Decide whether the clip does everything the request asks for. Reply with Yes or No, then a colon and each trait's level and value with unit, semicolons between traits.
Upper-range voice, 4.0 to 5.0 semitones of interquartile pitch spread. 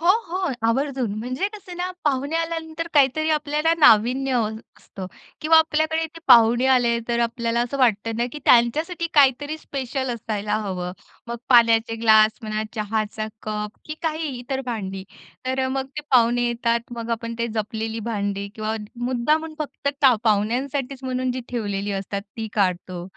Yes: high, 240 Hz; average, 4.5 semitones